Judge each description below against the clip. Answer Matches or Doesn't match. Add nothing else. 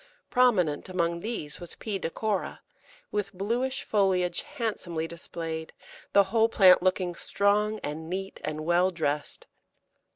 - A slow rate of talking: Matches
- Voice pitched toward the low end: Doesn't match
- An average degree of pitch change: Matches